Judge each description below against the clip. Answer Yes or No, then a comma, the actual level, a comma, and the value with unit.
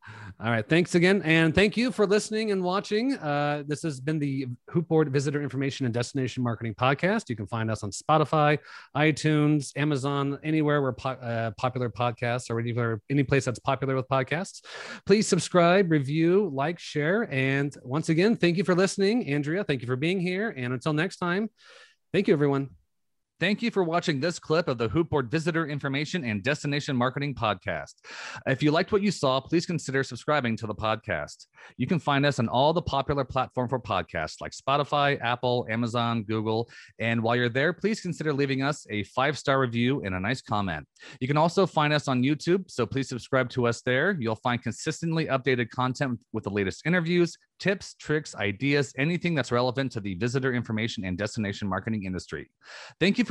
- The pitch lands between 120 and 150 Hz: Yes, medium, 140 Hz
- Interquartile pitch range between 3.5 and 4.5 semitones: No, average, 5.2 semitones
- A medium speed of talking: Yes, average, 190 wpm